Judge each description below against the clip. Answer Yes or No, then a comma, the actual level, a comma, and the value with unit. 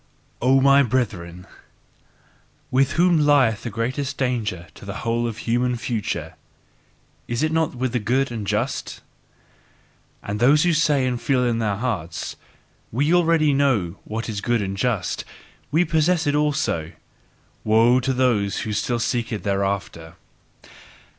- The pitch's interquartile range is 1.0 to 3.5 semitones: No, average, 4.7 semitones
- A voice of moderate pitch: No, low, 120 Hz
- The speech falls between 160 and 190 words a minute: No, average, 140 wpm